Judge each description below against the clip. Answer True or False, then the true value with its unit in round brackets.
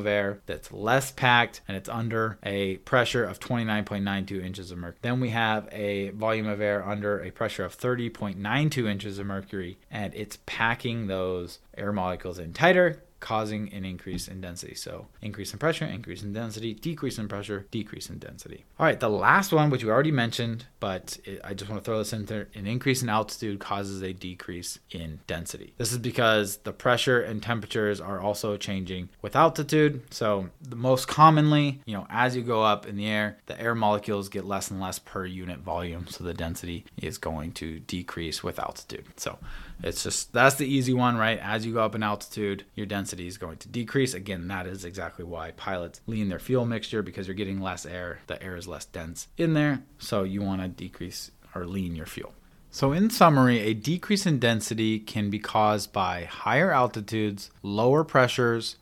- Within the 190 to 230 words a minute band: True (195 wpm)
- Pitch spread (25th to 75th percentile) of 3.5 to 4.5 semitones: True (3.9 semitones)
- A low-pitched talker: True (105 Hz)